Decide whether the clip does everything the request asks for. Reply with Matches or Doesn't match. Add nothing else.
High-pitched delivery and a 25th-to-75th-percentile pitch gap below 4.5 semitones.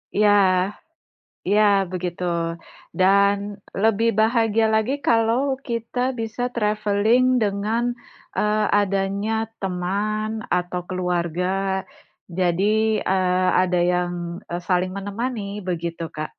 Matches